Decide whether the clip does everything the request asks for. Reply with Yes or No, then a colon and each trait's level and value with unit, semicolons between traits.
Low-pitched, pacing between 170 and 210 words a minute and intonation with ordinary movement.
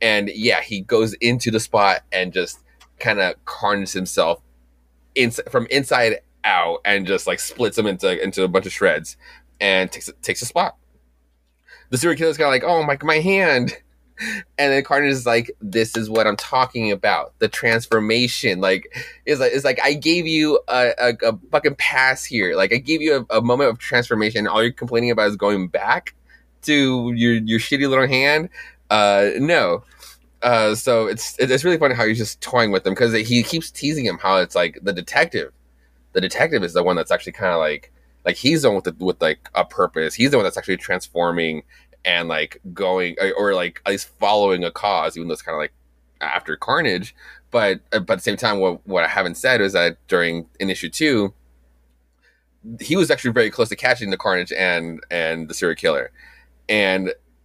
No: low, 110 Hz; average, 200 wpm; wide, 7.3 semitones